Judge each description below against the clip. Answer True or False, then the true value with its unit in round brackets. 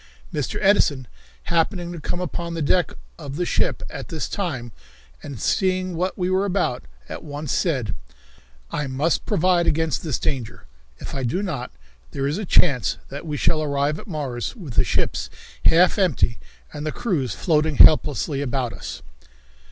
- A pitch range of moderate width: True (4.4 semitones)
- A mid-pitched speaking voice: True (155 Hz)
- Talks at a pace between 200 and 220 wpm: False (165 wpm)